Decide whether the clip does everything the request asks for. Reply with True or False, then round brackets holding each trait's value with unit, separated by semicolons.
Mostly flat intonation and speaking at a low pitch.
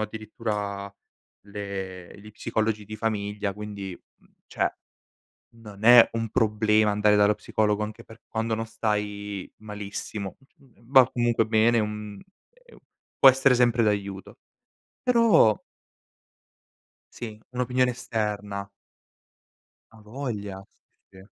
True (1.9 semitones; 105 Hz)